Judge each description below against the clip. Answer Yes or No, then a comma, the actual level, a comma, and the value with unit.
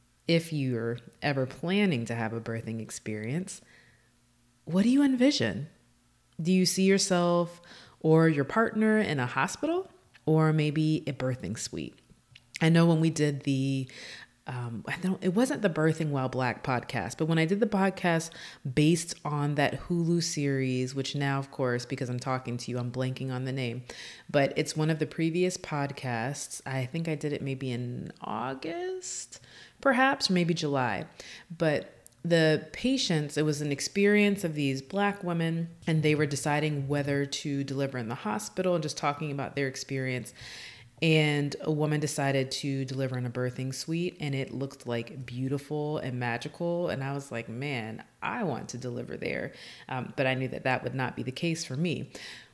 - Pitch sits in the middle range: Yes, medium, 145 Hz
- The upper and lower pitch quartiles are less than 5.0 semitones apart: Yes, average, 4.4 semitones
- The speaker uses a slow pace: No, average, 175 wpm